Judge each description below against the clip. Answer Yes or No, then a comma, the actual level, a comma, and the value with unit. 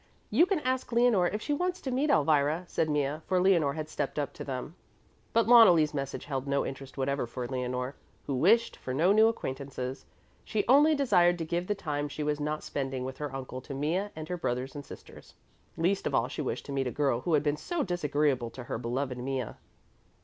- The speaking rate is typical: No, fast, 215 wpm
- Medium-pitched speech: Yes, medium, 150 Hz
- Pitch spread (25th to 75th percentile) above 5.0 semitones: Yes, wide, 5.4 semitones